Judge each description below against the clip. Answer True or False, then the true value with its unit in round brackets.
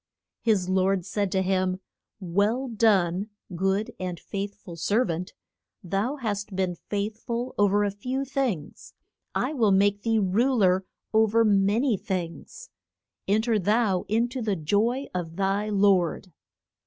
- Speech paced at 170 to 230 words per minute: False (155 wpm)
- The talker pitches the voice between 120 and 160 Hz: False (200 Hz)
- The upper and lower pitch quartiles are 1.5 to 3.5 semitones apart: True (3.1 semitones)